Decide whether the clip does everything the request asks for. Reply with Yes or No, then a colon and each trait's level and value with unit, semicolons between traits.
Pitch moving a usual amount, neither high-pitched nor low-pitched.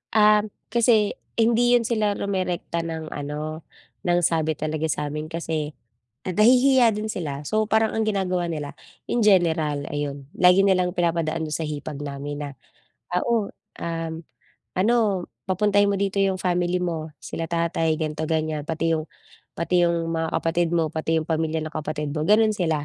Yes: average, 4.3 semitones; medium, 170 Hz